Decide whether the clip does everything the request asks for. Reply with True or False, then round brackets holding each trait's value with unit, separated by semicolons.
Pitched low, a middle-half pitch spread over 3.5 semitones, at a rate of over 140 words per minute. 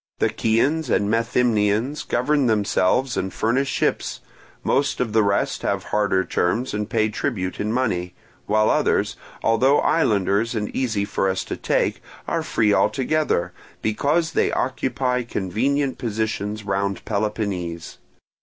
False (110 Hz; 4.0 semitones; 135 wpm)